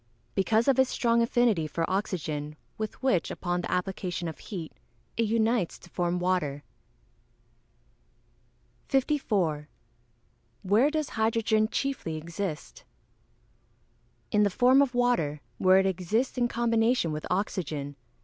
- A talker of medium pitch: No, high, 200 Hz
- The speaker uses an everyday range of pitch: No, wide, 5.7 semitones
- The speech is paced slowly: Yes, slow, 125 wpm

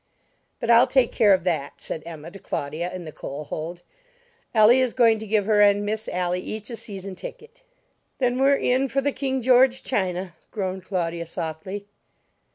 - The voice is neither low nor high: No, high, 205 Hz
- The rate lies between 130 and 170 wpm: No, average, 180 wpm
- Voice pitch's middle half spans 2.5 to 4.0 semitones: No, wide, 5.6 semitones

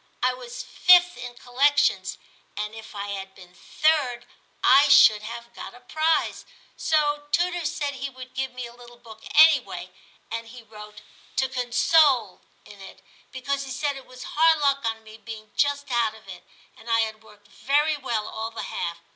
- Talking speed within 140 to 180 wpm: No, average, 190 wpm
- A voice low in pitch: No, high, 245 Hz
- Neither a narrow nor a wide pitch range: Yes, average, 4.5 semitones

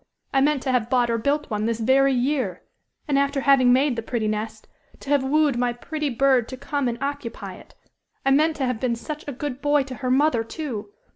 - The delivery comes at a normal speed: No, fast, 225 wpm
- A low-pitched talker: No, very high, 265 Hz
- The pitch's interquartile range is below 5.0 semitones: Yes, average, 3.1 semitones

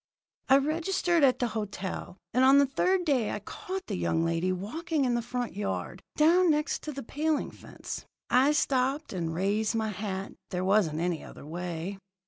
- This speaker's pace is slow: No, average, 180 wpm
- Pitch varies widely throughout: Yes, wide, 7.8 semitones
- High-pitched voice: Yes, high, 240 Hz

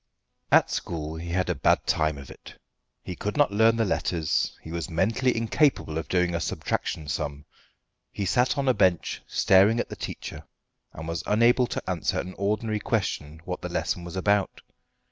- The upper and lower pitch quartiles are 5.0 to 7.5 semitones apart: Yes, wide, 5.5 semitones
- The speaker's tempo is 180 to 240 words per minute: Yes, average, 185 wpm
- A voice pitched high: No, very low, 95 Hz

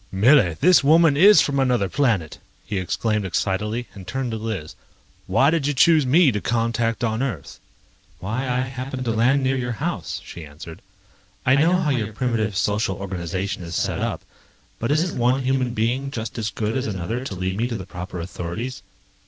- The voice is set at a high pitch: No, low, 115 Hz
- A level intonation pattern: No, average, 5.3 semitones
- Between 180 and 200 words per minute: Yes, average, 185 wpm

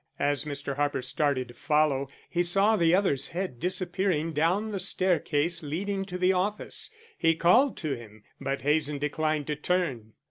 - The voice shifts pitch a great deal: No, average, 4.2 semitones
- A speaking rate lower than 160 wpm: No, average, 165 wpm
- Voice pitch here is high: No, medium, 160 Hz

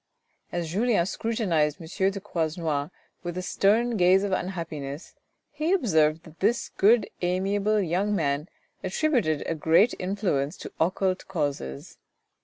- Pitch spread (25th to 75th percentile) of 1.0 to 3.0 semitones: No, average, 4.3 semitones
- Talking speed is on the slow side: Yes, slow, 130 wpm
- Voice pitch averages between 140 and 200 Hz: Yes, medium, 185 Hz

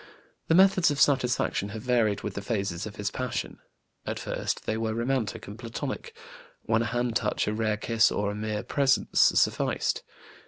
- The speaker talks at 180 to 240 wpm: No, average, 170 wpm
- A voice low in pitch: Yes, low, 115 Hz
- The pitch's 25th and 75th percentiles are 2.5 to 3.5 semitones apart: Yes, average, 3.2 semitones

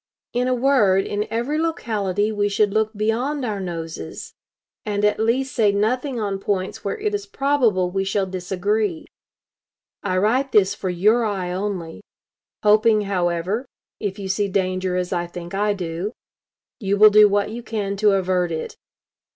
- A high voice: Yes, high, 205 Hz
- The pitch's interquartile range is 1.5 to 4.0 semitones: Yes, average, 2.9 semitones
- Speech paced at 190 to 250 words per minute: No, average, 165 wpm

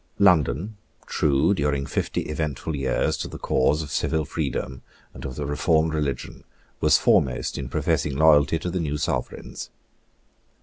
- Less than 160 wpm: Yes, average, 145 wpm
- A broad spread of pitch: No, narrow, 2.6 semitones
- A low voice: Yes, very low, 75 Hz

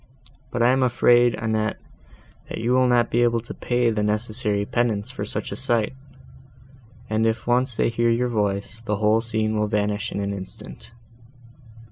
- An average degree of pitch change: No, narrow, 2.2 semitones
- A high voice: No, low, 115 Hz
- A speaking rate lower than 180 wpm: Yes, average, 170 wpm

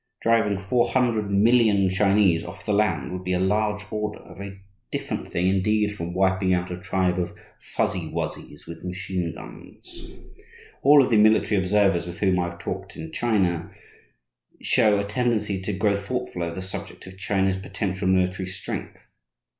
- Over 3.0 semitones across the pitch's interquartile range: No, narrow, 2.4 semitones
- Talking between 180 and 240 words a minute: No, average, 170 wpm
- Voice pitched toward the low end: Yes, very low, 95 Hz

